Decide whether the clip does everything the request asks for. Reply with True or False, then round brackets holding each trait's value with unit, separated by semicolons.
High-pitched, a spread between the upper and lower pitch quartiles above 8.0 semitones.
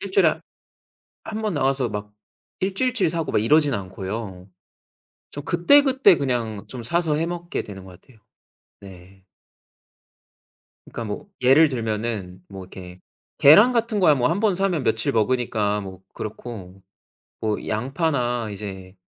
False (120 Hz; 8.4 semitones)